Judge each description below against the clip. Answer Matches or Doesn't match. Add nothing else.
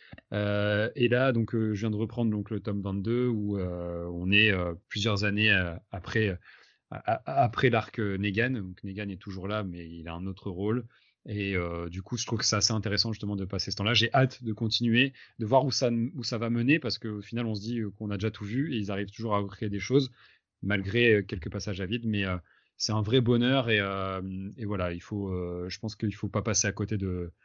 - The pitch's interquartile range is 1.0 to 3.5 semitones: Matches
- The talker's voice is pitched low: Matches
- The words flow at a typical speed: Doesn't match